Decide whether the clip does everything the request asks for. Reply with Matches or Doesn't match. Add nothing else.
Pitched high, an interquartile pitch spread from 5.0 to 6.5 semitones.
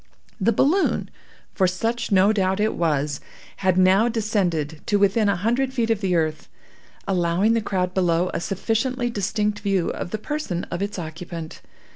Doesn't match